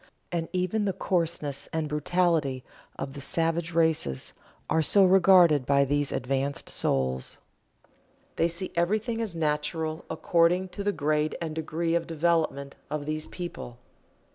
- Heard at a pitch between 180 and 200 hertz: No, medium, 160 Hz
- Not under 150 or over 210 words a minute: No, average, 140 wpm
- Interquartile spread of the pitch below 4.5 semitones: Yes, average, 3.1 semitones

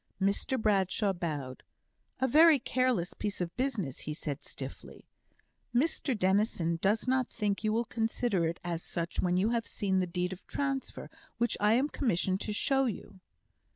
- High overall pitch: Yes, high, 205 Hz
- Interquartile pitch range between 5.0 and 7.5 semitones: Yes, average, 5.3 semitones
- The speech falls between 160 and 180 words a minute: Yes, average, 165 wpm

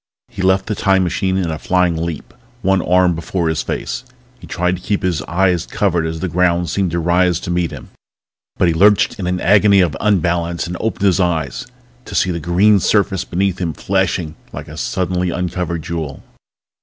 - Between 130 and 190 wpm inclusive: No, average, 200 wpm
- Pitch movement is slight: Yes, narrow, 1.9 semitones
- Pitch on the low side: Yes, very low, 90 Hz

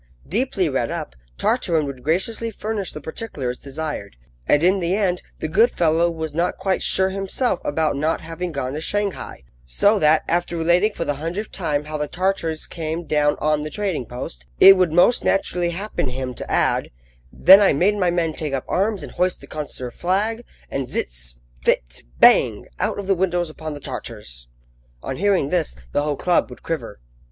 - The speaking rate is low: No, average, 185 wpm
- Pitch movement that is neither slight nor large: Yes, average, 4.6 semitones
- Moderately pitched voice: Yes, medium, 165 Hz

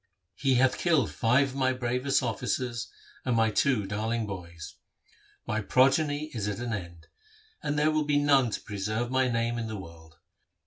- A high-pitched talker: No, low, 120 Hz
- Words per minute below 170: No, average, 175 wpm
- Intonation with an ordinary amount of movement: Yes, average, 4.2 semitones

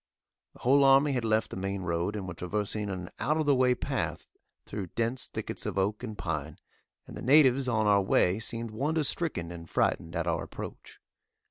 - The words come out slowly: No, average, 200 wpm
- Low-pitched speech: Yes, low, 110 Hz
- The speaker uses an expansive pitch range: Yes, wide, 5.9 semitones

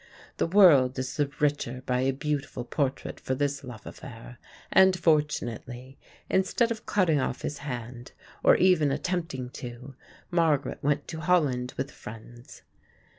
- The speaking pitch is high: No, medium, 140 Hz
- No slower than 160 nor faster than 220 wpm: No, average, 140 wpm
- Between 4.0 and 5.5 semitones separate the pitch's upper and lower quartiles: Yes, average, 4.3 semitones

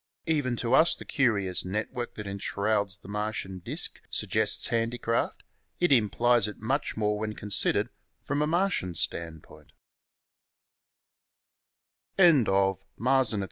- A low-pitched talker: Yes, low, 110 Hz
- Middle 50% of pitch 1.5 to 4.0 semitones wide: Yes, average, 3.6 semitones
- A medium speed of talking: No, slow, 110 wpm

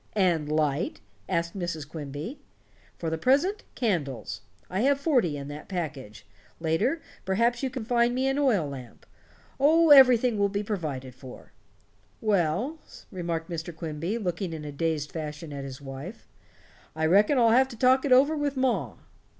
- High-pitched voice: No, medium, 180 Hz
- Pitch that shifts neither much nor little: No, wide, 8.5 semitones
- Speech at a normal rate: Yes, average, 160 wpm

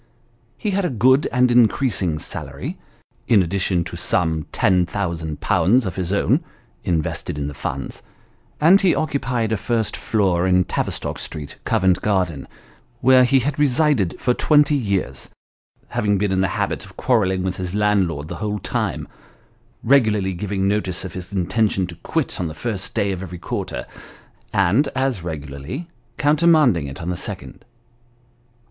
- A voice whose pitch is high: No, low, 100 Hz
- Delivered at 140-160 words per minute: Yes, average, 155 wpm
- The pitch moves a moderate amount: No, wide, 5.8 semitones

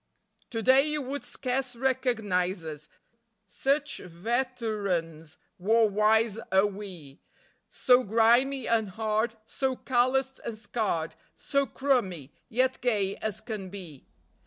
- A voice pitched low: No, high, 220 Hz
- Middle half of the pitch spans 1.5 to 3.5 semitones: No, average, 5.1 semitones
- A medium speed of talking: No, slow, 120 wpm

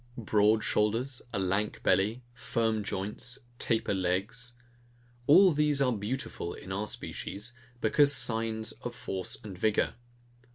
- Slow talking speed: Yes, slow, 125 wpm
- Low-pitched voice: Yes, low, 110 Hz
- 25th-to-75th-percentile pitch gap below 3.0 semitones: No, average, 3.6 semitones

